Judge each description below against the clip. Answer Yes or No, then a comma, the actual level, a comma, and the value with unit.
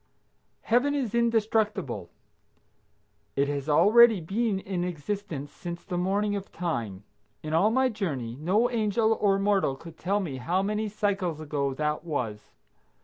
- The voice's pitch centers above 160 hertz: Yes, high, 190 Hz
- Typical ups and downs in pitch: No, wide, 5.9 semitones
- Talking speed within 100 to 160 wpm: Yes, average, 145 wpm